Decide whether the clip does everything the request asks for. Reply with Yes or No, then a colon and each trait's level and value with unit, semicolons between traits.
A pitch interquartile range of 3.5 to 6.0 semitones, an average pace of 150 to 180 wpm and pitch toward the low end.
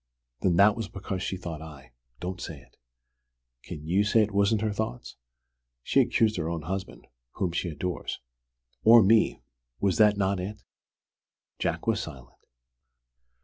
Yes: average, 4.2 semitones; average, 155 wpm; very low, 95 Hz